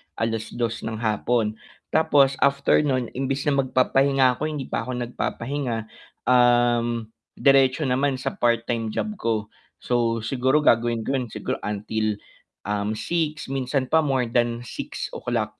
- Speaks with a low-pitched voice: Yes, low, 125 Hz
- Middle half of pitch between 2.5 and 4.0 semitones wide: Yes, average, 2.9 semitones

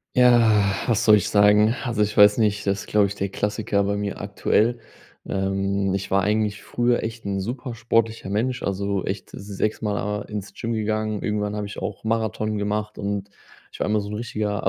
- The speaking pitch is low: Yes, low, 105 Hz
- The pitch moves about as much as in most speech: No, narrow, 1.6 semitones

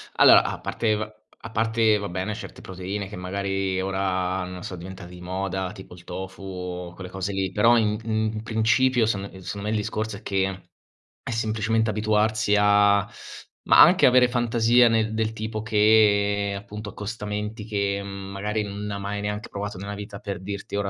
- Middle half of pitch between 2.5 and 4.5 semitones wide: No, narrow, 2.1 semitones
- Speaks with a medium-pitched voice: No, low, 105 Hz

